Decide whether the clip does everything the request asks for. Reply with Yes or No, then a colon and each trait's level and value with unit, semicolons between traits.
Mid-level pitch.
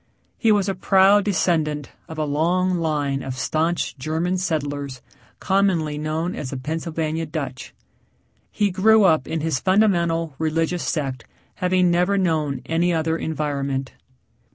Yes: medium, 160 Hz